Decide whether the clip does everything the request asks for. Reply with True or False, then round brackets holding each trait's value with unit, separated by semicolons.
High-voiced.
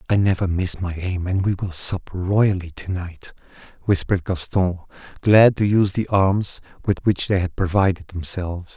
False (95 Hz)